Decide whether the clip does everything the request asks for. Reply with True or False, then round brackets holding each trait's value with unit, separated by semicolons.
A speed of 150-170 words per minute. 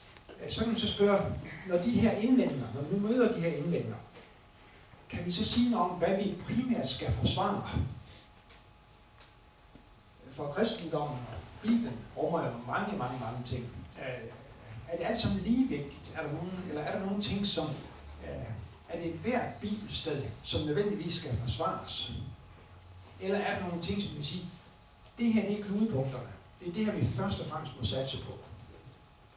True (165 wpm)